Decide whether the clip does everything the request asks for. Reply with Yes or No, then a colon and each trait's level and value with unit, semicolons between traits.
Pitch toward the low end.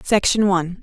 No: high, 190 Hz